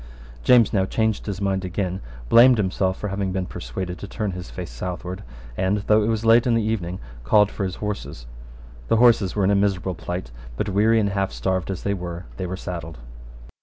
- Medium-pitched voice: No, very low, 95 Hz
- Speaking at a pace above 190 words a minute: Yes, fast, 205 wpm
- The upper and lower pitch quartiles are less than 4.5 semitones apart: Yes, narrow, 2.6 semitones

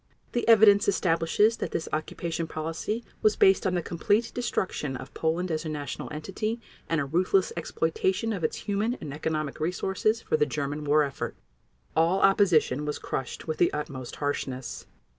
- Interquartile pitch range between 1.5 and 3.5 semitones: No, average, 4.7 semitones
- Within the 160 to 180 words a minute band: Yes, average, 165 wpm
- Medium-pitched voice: Yes, medium, 165 Hz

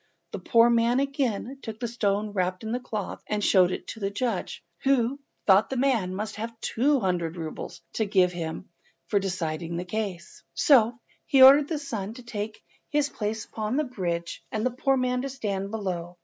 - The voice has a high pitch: Yes, high, 220 Hz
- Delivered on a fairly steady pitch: No, average, 4.8 semitones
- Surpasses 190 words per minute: Yes, average, 200 wpm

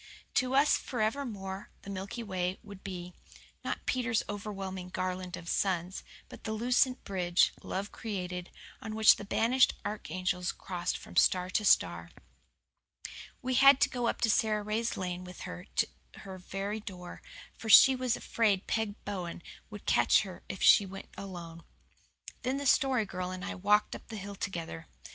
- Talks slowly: No, average, 160 wpm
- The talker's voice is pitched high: Yes, high, 195 Hz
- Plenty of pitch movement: No, average, 3.4 semitones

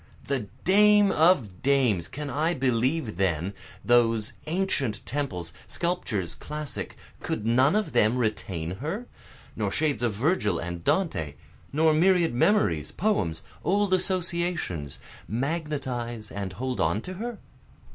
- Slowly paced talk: Yes, slow, 125 wpm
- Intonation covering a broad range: Yes, wide, 8.7 semitones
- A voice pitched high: No, low, 130 Hz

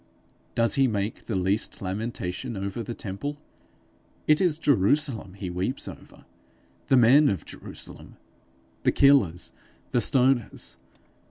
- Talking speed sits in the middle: No, slow, 120 wpm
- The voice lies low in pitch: Yes, low, 115 Hz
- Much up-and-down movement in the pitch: Yes, wide, 5.7 semitones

